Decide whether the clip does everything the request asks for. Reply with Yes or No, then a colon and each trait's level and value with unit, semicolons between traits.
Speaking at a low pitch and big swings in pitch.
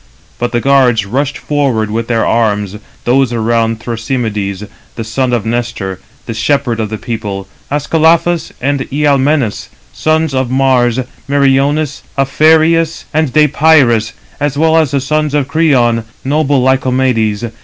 No: low, 130 Hz; average, 4.2 semitones